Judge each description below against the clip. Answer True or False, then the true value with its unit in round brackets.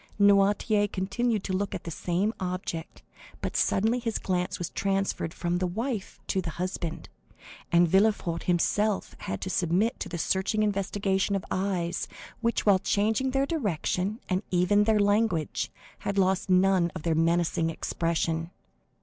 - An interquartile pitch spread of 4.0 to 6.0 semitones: False (3.0 semitones)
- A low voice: False (190 Hz)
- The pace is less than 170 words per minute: True (150 wpm)